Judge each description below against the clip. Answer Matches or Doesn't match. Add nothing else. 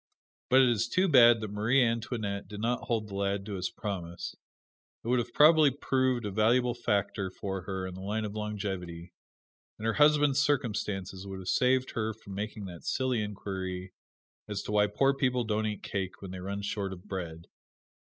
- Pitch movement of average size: Matches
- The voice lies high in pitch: Doesn't match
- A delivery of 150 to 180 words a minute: Doesn't match